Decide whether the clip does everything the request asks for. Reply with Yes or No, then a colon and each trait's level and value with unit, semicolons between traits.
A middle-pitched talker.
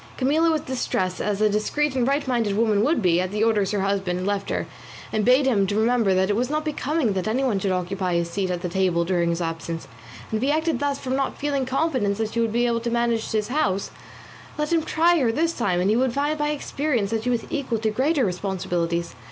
No: high, 225 Hz